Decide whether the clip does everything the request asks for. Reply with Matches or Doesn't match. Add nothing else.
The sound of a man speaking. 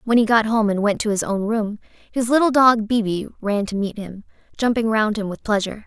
Doesn't match